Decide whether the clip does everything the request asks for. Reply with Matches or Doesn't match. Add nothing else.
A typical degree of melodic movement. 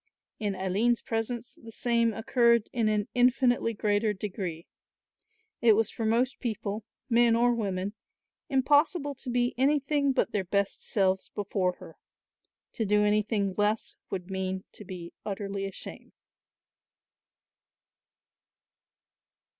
Matches